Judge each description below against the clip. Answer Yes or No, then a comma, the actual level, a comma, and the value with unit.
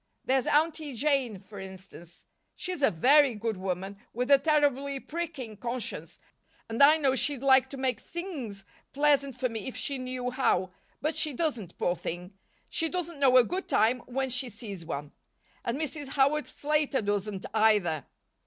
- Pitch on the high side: Yes, very high, 255 Hz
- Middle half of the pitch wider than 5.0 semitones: Yes, wide, 5.5 semitones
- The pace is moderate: Yes, average, 165 wpm